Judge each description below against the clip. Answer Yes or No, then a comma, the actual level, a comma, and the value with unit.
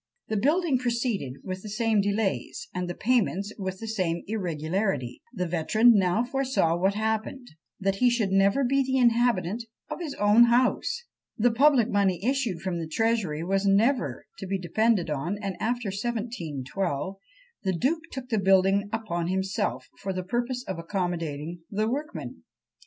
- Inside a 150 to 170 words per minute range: Yes, average, 160 wpm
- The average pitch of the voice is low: No, high, 205 Hz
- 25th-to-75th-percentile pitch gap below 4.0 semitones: No, average, 4.5 semitones